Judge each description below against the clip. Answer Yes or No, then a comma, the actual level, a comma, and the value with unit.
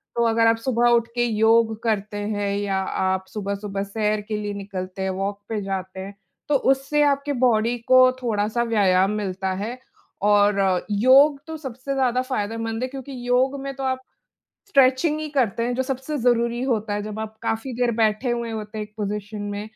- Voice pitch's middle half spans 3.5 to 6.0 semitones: Yes, average, 3.8 semitones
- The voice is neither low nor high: No, high, 225 Hz